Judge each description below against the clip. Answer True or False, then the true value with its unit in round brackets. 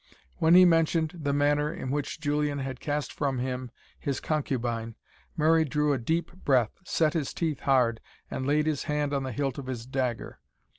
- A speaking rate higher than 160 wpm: True (185 wpm)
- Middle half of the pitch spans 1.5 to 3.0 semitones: True (2.7 semitones)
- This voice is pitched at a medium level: True (145 Hz)